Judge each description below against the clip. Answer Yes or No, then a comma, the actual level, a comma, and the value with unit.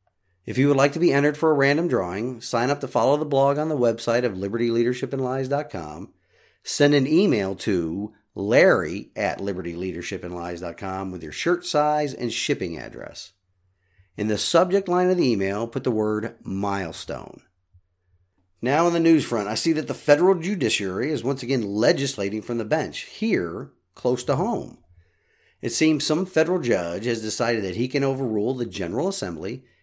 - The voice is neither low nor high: No, low, 120 Hz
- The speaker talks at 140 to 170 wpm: Yes, average, 165 wpm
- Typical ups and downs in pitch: No, wide, 6.7 semitones